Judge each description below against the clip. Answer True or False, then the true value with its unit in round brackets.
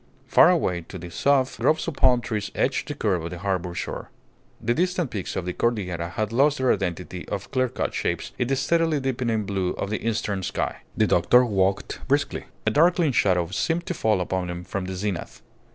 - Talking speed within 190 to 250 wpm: True (200 wpm)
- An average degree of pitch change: False (6.3 semitones)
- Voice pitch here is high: False (105 Hz)